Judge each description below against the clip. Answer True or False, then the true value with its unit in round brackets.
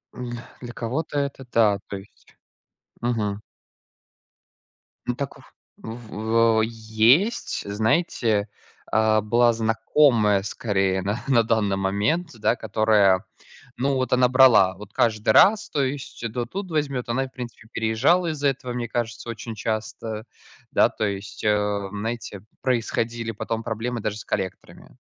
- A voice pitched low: True (115 Hz)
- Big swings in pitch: False (2.9 semitones)